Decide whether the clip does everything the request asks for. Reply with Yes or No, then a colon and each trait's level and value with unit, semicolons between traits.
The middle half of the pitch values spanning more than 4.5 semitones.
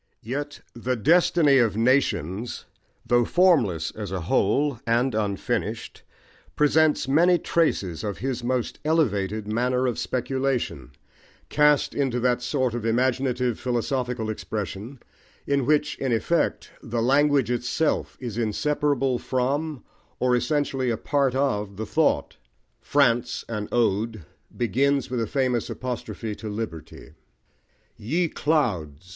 No: average, 4.2 semitones